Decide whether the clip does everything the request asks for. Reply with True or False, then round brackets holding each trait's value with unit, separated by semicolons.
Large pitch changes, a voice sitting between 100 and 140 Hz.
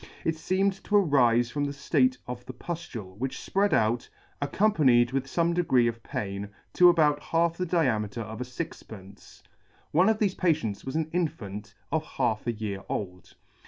True (7.2 semitones; 135 Hz)